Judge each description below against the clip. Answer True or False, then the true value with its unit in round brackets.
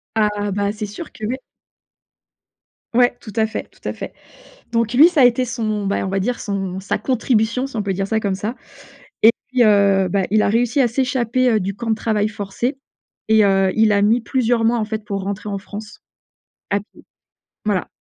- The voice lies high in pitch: True (215 Hz)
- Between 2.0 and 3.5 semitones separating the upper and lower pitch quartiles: True (2.9 semitones)